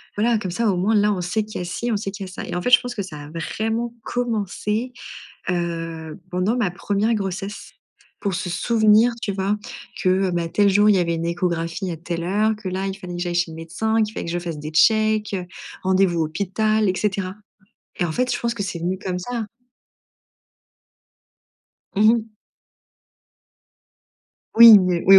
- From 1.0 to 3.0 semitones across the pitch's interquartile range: No, average, 3.6 semitones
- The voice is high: Yes, high, 195 Hz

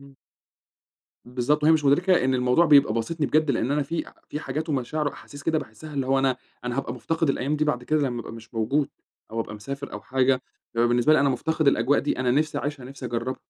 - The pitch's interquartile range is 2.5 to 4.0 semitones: Yes, average, 3.3 semitones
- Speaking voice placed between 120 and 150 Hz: Yes, low, 135 Hz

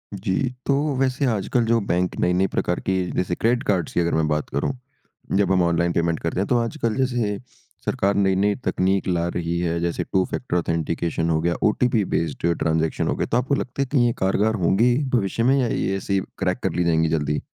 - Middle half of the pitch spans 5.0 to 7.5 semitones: Yes, average, 5.3 semitones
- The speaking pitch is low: Yes, very low, 95 Hz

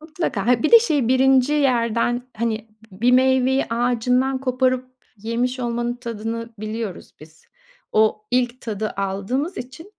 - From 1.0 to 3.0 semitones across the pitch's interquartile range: Yes, narrow, 2.5 semitones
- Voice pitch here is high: Yes, high, 245 Hz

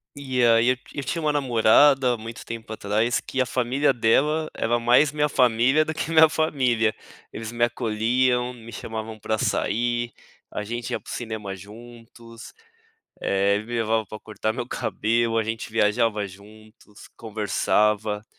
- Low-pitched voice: Yes, low, 115 Hz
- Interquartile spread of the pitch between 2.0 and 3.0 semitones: Yes, narrow, 2.5 semitones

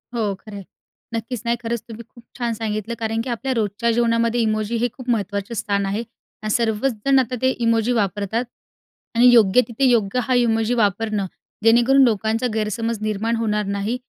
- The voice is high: Yes, high, 225 Hz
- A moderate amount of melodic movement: No, narrow, 2.0 semitones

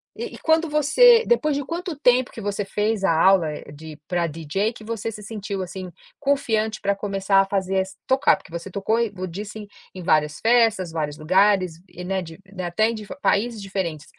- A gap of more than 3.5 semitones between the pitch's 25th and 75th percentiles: Yes, average, 4.2 semitones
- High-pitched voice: Yes, high, 200 Hz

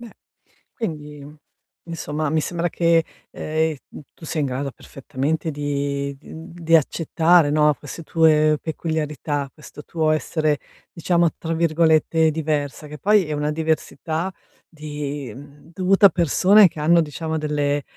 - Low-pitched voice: No, medium, 155 Hz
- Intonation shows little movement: Yes, narrow, 2.1 semitones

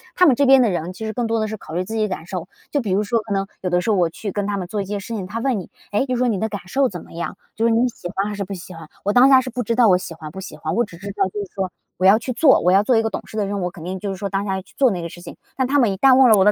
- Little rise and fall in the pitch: No, average, 3.9 semitones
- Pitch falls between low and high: No, high, 205 Hz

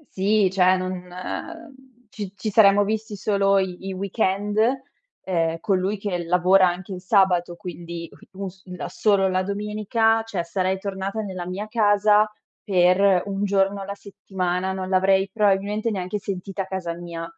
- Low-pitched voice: No, high, 195 Hz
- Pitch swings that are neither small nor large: No, narrow, 1.9 semitones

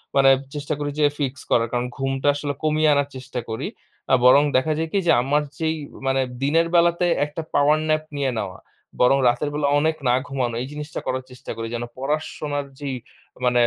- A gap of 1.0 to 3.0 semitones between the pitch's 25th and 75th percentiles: Yes, average, 2.7 semitones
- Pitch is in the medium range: Yes, medium, 145 Hz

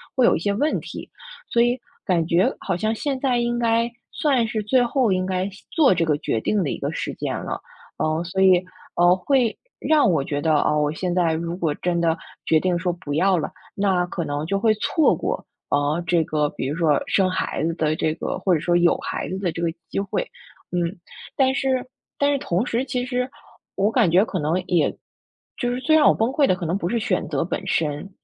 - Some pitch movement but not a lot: No, wide, 6.0 semitones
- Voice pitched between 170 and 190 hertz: Yes, medium, 185 Hz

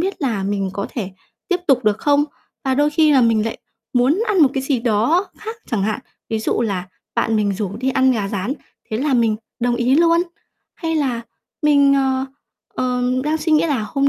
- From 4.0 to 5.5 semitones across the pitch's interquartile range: Yes, average, 5.2 semitones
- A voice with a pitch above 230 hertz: Yes, very high, 255 Hz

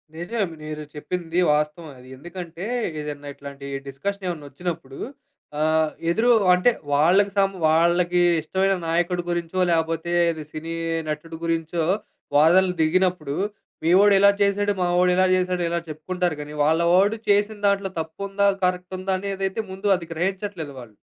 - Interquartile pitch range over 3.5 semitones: No, average, 3.2 semitones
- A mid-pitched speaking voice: Yes, medium, 175 Hz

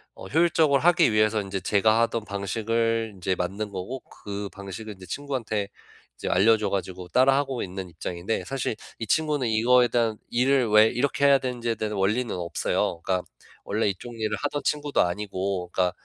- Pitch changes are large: No, average, 4.4 semitones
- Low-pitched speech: Yes, low, 110 Hz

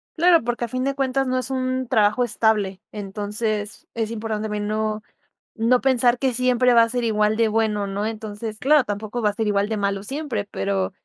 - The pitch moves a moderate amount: Yes, average, 3.2 semitones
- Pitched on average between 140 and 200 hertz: No, high, 220 Hz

